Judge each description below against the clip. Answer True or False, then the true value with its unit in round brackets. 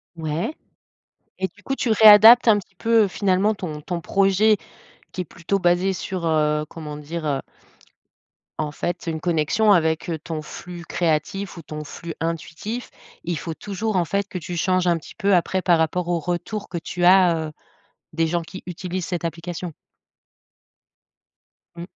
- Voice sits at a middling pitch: True (175 Hz)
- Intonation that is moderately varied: True (3.0 semitones)